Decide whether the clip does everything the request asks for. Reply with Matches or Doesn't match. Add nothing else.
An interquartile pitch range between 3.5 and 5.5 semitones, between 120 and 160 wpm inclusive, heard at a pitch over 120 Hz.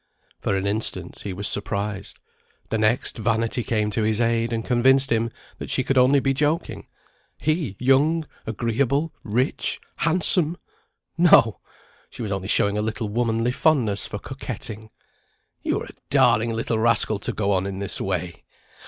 Doesn't match